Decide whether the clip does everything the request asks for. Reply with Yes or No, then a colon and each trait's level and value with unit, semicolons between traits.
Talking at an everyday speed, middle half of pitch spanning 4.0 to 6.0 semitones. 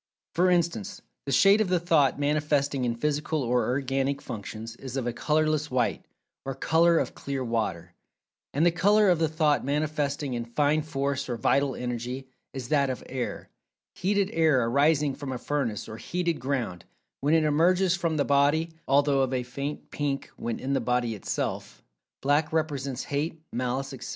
No: average, 170 wpm; average, 3.5 semitones